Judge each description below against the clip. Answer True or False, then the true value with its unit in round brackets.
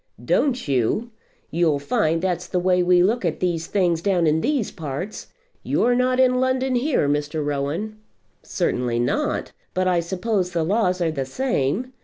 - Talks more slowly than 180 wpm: True (165 wpm)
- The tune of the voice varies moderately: False (6.6 semitones)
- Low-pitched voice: False (180 Hz)